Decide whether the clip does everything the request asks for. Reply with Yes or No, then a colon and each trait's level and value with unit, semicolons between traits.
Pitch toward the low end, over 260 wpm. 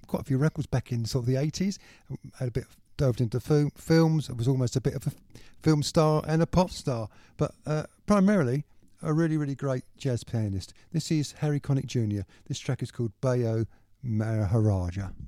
No: low, 130 Hz; average, 200 wpm